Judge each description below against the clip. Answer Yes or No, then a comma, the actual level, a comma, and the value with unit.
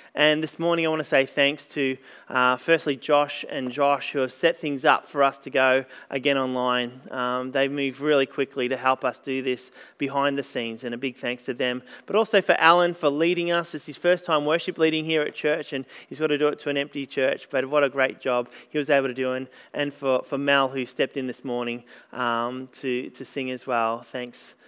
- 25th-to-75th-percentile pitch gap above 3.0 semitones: No, narrow, 2.6 semitones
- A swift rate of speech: Yes, fast, 235 wpm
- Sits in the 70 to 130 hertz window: No, medium, 140 Hz